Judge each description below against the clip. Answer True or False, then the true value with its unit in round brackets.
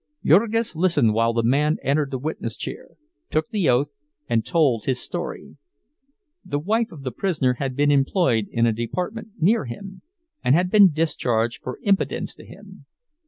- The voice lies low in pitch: False (145 Hz)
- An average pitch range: False (6.7 semitones)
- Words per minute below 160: False (165 wpm)